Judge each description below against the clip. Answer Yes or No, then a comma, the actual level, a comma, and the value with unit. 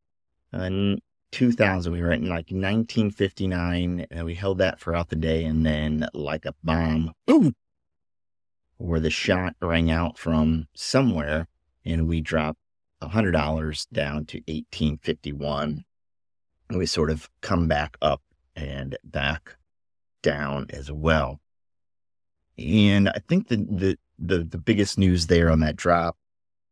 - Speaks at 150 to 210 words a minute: No, average, 140 wpm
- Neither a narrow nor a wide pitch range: Yes, average, 3.9 semitones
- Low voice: Yes, very low, 85 Hz